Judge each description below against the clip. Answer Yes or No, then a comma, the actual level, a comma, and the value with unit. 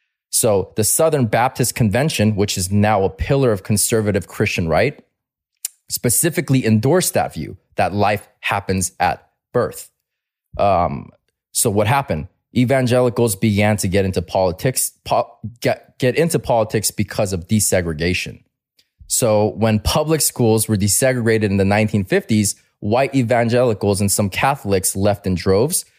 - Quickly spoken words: No, slow, 135 wpm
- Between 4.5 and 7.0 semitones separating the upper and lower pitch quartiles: No, average, 3.4 semitones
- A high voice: No, low, 110 Hz